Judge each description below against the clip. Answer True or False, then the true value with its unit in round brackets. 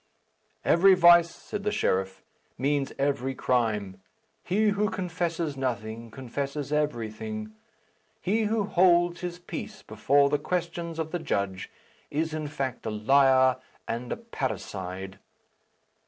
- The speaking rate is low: True (125 wpm)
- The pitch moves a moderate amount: False (6.2 semitones)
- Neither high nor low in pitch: True (145 Hz)